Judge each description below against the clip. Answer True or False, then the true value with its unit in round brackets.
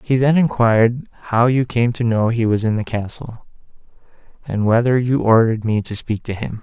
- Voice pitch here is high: False (115 Hz)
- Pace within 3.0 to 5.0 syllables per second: False (5.3 syllables/s)